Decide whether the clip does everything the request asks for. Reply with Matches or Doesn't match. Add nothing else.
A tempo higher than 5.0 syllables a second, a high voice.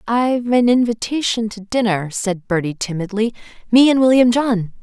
Doesn't match